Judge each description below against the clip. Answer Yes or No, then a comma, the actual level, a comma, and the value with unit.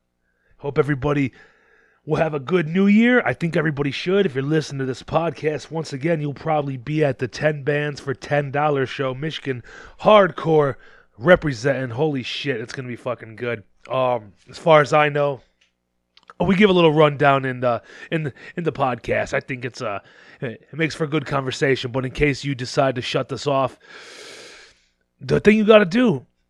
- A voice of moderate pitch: Yes, medium, 145 Hz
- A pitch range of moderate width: Yes, average, 3.8 semitones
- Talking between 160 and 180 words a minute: No, average, 190 wpm